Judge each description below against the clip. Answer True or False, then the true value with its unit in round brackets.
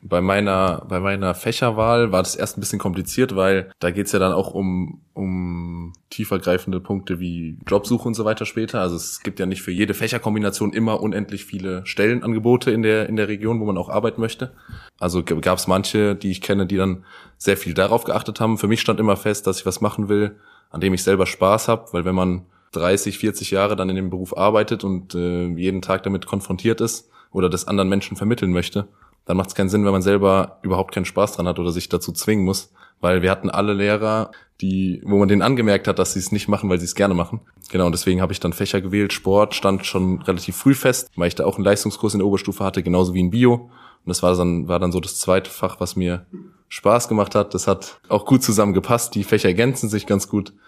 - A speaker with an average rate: False (235 wpm)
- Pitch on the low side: True (100 Hz)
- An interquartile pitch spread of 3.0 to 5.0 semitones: False (2.4 semitones)